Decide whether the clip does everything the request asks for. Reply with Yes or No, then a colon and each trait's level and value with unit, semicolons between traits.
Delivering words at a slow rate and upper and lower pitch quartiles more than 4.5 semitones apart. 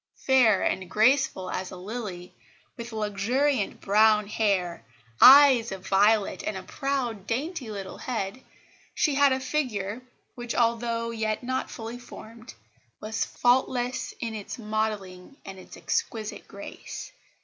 No: slow, 130 wpm; average, 3.7 semitones